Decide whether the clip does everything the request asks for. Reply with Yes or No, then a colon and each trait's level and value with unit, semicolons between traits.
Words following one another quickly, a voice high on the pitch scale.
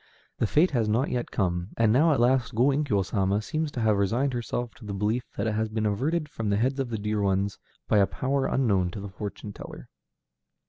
No: fast, 230 wpm; low, 110 Hz